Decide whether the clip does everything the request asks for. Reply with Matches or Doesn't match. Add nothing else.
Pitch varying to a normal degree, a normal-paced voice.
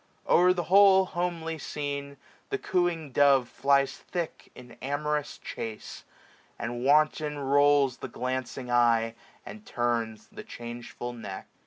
Doesn't match